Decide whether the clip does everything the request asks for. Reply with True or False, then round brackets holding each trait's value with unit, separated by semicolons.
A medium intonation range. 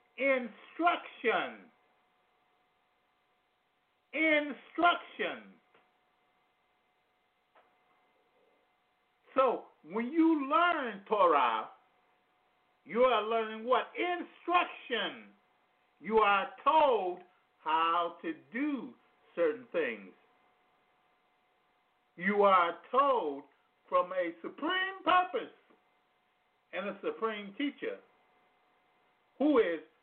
False (7.9 semitones)